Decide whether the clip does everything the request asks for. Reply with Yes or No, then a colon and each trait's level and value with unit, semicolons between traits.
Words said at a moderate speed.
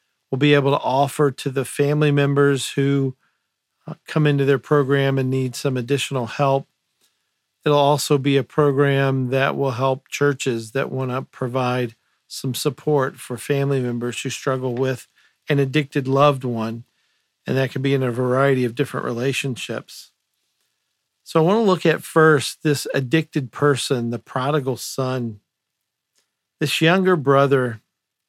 Yes: average, 150 wpm